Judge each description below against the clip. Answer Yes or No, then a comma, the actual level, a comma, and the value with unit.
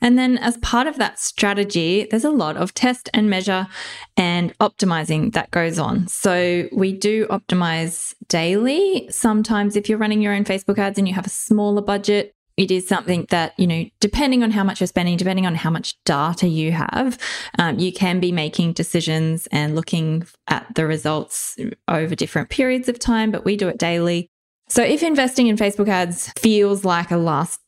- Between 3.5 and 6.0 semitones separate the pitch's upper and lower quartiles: Yes, average, 4.0 semitones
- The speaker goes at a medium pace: Yes, average, 190 wpm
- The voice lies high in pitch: Yes, high, 195 Hz